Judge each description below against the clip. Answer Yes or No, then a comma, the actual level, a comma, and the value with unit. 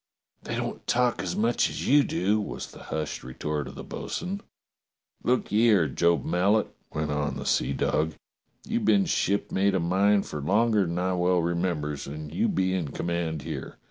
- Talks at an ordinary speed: Yes, average, 175 wpm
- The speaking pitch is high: No, very low, 90 Hz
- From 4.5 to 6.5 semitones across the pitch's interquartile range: Yes, average, 5.1 semitones